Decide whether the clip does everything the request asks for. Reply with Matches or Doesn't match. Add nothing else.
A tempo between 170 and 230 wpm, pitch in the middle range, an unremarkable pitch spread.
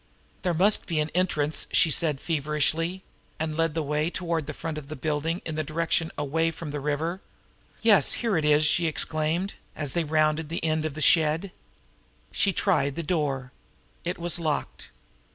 Doesn't match